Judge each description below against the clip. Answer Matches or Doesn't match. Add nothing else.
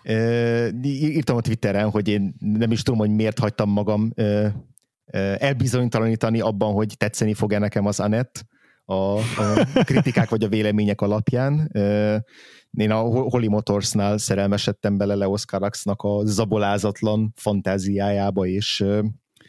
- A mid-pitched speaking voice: Doesn't match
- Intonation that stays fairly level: Matches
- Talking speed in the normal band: Matches